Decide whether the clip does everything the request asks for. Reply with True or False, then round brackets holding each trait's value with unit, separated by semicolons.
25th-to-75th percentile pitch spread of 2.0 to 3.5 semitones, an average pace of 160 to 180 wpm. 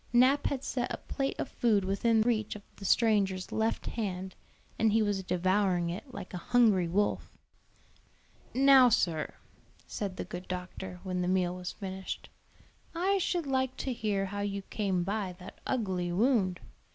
False (4.2 semitones; 165 wpm)